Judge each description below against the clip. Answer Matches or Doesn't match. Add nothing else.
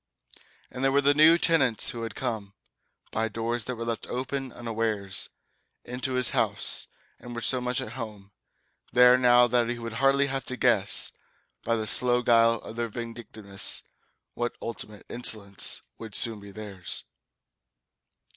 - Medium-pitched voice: Doesn't match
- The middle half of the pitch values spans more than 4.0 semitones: Doesn't match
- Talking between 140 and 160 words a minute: Matches